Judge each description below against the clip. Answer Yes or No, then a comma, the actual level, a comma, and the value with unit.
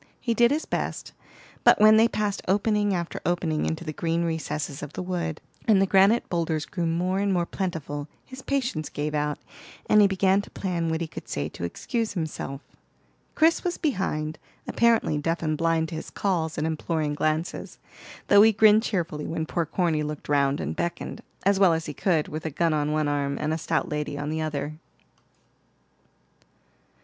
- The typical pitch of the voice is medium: Yes, medium, 165 Hz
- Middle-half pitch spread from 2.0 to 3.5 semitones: No, average, 4.2 semitones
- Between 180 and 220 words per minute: Yes, average, 190 wpm